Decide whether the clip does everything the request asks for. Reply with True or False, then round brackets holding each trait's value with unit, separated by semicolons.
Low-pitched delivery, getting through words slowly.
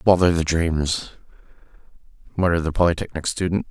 True (85 Hz; 115 wpm)